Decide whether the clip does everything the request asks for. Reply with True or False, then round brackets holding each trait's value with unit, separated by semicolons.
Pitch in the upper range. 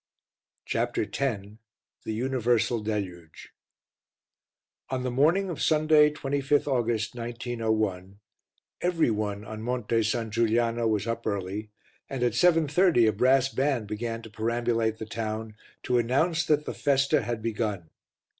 False (115 Hz)